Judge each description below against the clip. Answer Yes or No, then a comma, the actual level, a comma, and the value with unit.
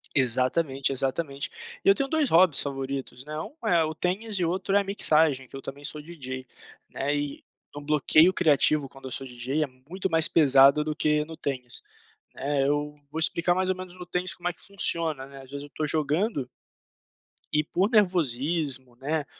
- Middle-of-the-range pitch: Yes, medium, 150 Hz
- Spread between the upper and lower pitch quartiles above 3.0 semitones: Yes, average, 4.3 semitones